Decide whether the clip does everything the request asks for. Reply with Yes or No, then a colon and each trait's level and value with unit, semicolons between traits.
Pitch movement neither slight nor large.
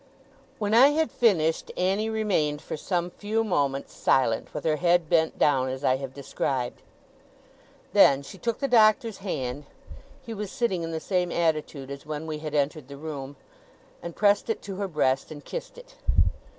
No: wide, 6.5 semitones